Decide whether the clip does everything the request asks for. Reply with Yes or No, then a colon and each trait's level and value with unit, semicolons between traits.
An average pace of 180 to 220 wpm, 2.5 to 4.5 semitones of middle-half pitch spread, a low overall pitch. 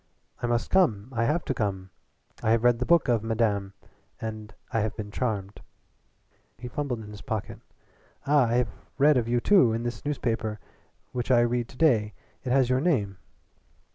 Yes: average, 185 wpm; average, 3.0 semitones; low, 120 Hz